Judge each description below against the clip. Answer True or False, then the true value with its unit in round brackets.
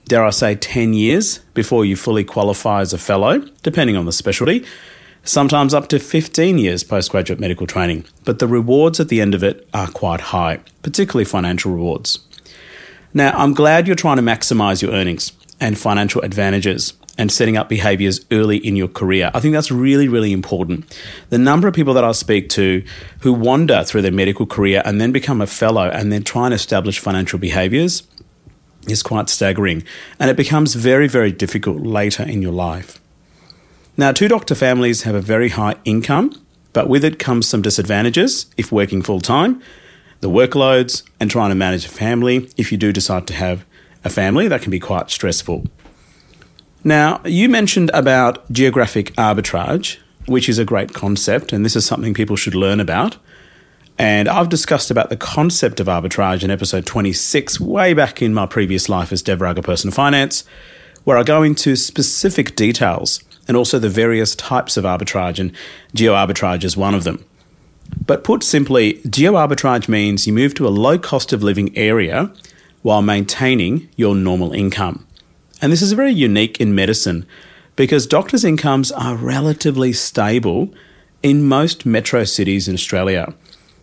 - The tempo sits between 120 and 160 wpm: False (175 wpm)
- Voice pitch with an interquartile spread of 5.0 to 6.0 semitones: True (5.5 semitones)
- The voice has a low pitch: True (110 Hz)